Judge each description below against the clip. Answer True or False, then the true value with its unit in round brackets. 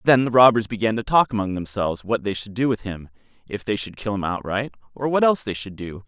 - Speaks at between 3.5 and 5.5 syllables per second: False (6.2 syllables/s)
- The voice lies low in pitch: True (105 Hz)